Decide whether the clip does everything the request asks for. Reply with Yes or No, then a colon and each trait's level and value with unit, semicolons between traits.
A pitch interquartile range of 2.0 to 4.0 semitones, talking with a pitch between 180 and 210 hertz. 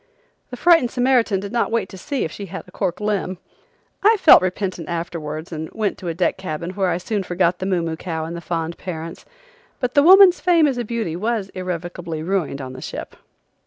No: wide, 5.6 semitones; medium, 185 Hz